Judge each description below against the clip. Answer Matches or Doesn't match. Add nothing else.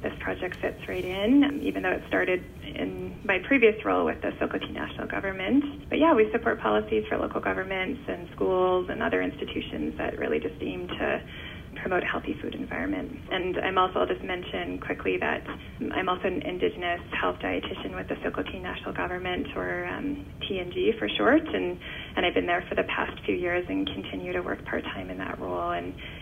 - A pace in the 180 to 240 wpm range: Matches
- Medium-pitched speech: Matches